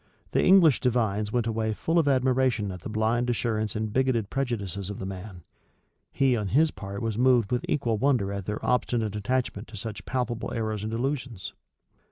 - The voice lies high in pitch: No, low, 115 Hz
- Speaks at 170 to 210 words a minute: Yes, average, 185 wpm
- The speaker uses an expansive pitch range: No, average, 3.4 semitones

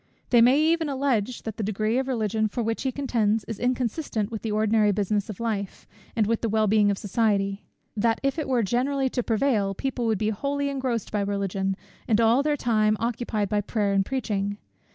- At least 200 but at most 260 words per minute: Yes, fast, 205 wpm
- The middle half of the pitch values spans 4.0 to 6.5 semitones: No, average, 3.4 semitones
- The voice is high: Yes, high, 220 Hz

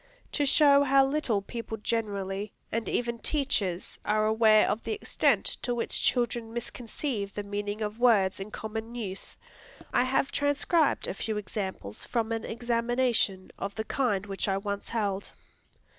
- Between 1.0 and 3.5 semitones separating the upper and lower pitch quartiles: Yes, average, 3.2 semitones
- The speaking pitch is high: Yes, high, 220 Hz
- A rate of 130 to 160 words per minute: Yes, average, 155 wpm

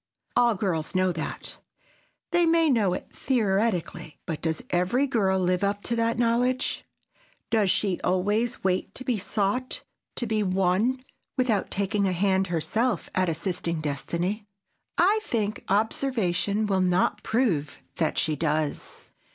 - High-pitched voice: Yes, high, 200 Hz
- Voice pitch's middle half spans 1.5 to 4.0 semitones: No, average, 4.4 semitones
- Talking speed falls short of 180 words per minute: Yes, average, 140 wpm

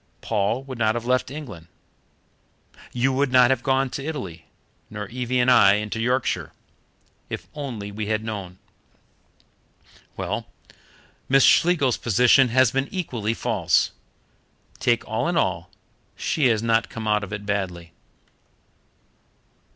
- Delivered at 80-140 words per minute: Yes, slow, 135 wpm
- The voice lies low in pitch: Yes, low, 120 Hz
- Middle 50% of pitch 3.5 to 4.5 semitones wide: Yes, average, 3.9 semitones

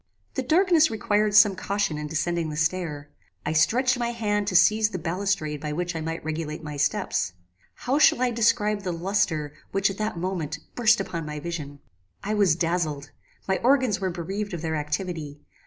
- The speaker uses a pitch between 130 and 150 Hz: No, medium, 180 Hz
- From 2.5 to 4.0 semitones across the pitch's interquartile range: No, average, 5.1 semitones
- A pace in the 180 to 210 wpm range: Yes, average, 185 wpm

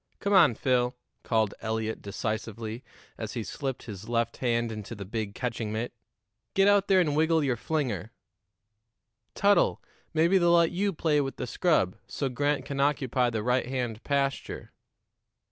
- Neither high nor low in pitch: No, low, 125 Hz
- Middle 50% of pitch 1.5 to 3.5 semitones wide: No, average, 5.1 semitones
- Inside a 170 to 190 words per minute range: No, average, 160 wpm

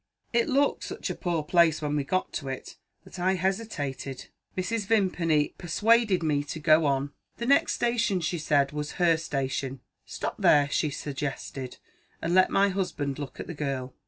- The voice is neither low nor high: Yes, medium, 160 Hz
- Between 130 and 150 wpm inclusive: No, average, 175 wpm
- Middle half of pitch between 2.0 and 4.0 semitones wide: No, average, 4.7 semitones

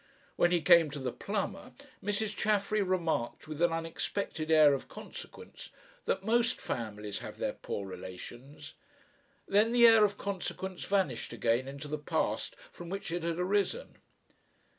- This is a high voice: No, medium, 170 Hz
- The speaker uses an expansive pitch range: Yes, wide, 6.2 semitones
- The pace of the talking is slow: No, average, 150 wpm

